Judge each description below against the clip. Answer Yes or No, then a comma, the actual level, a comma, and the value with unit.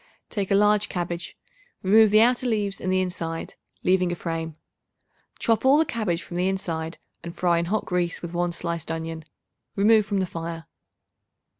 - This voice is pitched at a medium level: Yes, medium, 180 Hz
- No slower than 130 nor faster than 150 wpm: No, average, 175 wpm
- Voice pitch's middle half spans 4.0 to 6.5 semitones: No, average, 3.5 semitones